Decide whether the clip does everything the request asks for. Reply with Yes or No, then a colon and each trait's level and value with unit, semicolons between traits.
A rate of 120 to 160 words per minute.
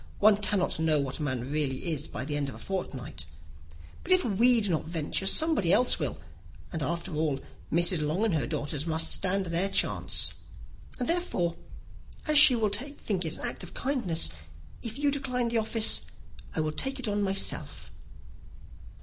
No: average, 180 wpm